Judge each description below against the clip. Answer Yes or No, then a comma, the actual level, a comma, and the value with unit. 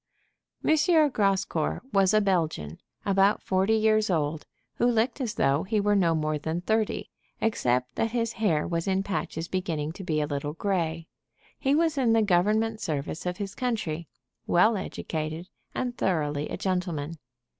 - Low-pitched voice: No, medium, 185 Hz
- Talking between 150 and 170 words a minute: Yes, average, 160 wpm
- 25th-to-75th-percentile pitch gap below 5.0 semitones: No, wide, 5.4 semitones